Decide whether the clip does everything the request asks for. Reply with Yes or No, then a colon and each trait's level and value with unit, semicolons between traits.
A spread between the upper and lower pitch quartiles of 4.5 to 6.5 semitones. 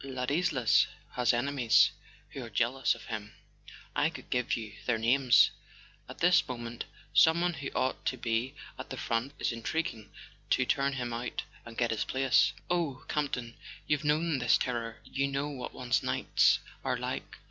No: average, 3.0 semitones